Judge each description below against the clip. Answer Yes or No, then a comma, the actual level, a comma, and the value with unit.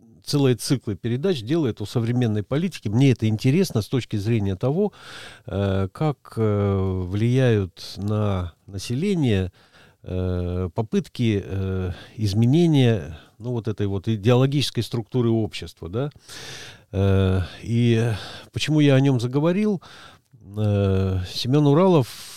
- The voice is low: Yes, low, 115 Hz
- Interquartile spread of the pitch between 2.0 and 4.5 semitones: No, average, 4.9 semitones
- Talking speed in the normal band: No, slow, 95 wpm